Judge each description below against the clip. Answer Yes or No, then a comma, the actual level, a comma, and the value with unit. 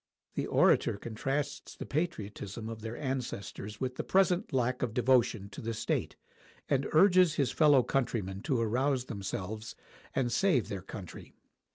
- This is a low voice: Yes, low, 125 Hz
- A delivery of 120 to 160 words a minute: Yes, average, 150 wpm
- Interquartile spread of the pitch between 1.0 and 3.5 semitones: No, average, 4.5 semitones